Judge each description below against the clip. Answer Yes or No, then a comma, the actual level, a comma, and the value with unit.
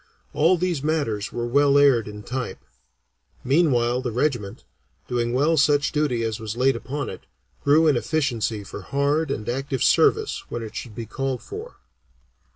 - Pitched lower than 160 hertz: Yes, low, 135 Hz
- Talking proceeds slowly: No, average, 160 wpm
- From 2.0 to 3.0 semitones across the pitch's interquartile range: No, average, 3.8 semitones